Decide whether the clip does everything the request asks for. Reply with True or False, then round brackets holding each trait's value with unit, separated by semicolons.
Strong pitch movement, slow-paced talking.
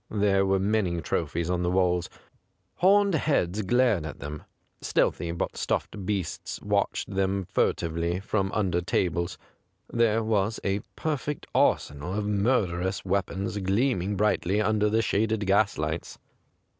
False (3.4 semitones; 130 wpm)